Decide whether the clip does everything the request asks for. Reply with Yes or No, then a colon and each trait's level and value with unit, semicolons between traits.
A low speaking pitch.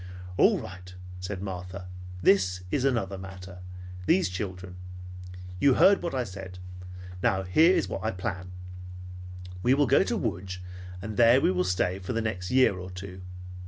Yes: very low, 95 Hz